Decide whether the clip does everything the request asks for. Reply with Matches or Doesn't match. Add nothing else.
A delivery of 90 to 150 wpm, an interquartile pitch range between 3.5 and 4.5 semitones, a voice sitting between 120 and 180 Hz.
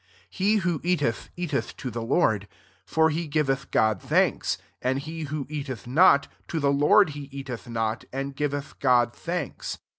Doesn't match